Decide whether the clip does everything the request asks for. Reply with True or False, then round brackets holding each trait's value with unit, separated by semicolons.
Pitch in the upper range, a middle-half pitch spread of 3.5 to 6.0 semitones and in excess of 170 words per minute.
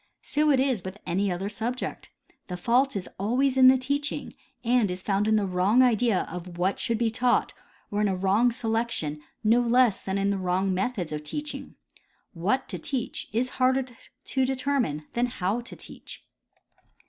True (225 Hz; 5.1 semitones; 180 wpm)